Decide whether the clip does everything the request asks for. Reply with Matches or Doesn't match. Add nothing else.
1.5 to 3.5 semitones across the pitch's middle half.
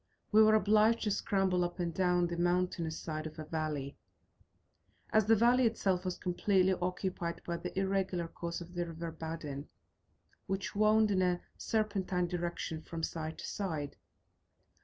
Matches